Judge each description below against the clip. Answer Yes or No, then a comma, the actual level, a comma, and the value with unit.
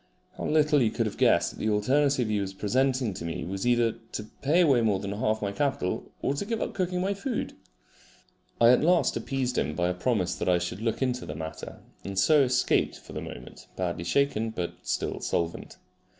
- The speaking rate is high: Yes, fast, 210 wpm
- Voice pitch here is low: Yes, low, 115 Hz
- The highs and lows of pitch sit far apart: Yes, wide, 6.4 semitones